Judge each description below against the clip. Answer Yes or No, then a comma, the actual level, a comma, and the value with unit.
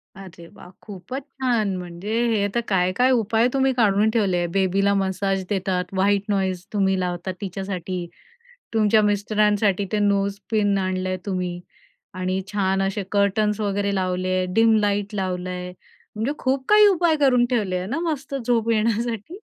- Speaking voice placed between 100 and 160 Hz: No, high, 200 Hz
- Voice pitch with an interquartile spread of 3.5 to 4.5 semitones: No, average, 3.0 semitones